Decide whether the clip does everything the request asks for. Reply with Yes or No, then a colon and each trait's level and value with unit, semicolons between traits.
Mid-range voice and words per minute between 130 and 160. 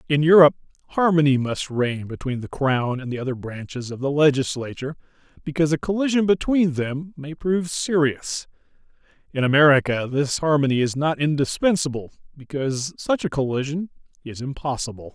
Yes: medium, 145 Hz; average, 145 wpm